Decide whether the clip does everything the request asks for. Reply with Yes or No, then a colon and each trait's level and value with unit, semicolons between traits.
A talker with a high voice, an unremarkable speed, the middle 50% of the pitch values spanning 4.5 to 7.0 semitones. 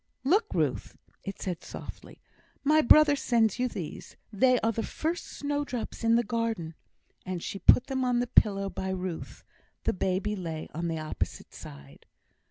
Yes: high, 225 Hz; average, 165 wpm; wide, 5.5 semitones